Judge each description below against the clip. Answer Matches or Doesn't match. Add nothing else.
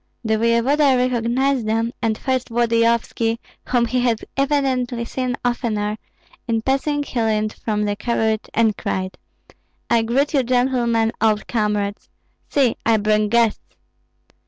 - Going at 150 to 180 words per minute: Doesn't match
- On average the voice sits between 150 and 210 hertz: Doesn't match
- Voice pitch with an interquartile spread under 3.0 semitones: Matches